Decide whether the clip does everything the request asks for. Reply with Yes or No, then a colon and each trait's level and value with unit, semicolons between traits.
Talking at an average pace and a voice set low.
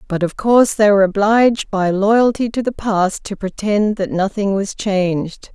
No: average, 185 wpm; high, 205 Hz